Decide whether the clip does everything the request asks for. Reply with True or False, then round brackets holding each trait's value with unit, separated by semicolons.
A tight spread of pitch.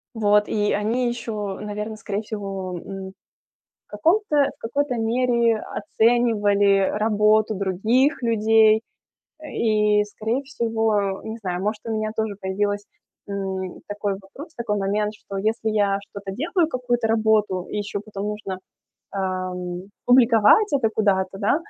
True (2.2 semitones)